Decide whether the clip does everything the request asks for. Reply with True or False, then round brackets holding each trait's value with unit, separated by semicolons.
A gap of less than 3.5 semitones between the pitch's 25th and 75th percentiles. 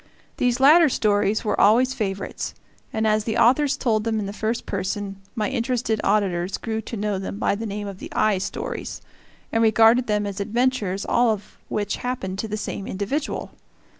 True (2.8 semitones)